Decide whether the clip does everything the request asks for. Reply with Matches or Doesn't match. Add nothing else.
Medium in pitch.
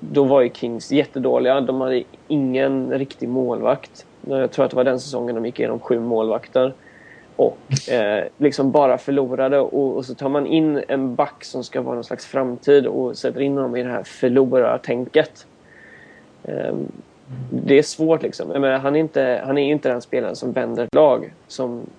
Doesn't match